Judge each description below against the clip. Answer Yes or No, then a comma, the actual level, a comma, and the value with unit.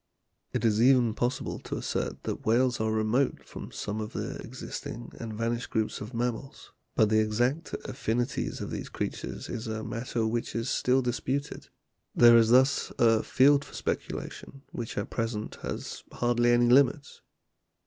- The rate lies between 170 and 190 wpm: No, average, 160 wpm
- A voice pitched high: No, low, 120 Hz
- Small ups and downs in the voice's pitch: Yes, narrow, 2.3 semitones